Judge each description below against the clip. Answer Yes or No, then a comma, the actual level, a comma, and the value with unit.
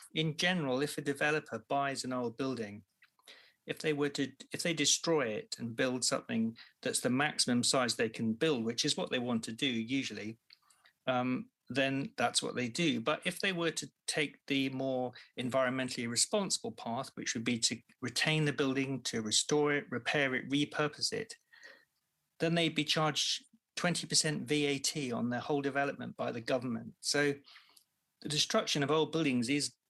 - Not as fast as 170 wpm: No, average, 175 wpm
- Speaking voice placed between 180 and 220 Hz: No, medium, 140 Hz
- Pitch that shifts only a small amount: No, average, 3.6 semitones